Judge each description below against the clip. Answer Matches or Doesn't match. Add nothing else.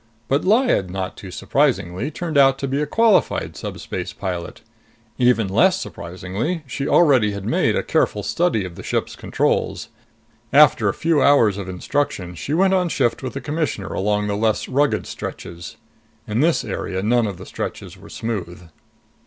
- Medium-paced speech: Matches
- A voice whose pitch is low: Matches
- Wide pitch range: Matches